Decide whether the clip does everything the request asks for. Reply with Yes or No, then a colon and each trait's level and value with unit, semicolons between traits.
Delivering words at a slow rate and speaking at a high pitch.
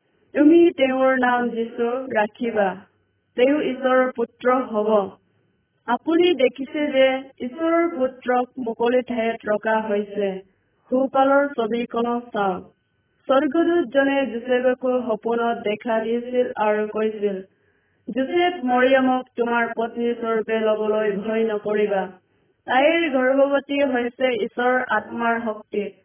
Yes: slow, 95 wpm; high, 240 Hz